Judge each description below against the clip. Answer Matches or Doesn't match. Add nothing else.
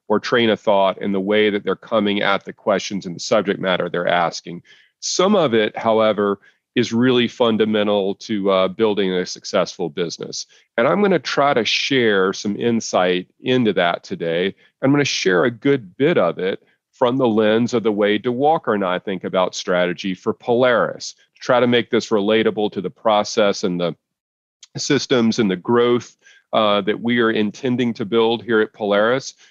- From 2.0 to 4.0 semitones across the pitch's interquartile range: Matches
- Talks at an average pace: Matches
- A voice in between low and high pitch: Doesn't match